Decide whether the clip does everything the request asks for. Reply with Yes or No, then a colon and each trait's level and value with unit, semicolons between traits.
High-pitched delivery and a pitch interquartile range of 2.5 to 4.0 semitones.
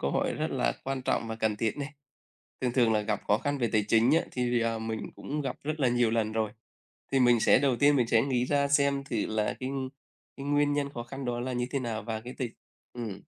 No: low, 120 Hz; average, 3.6 semitones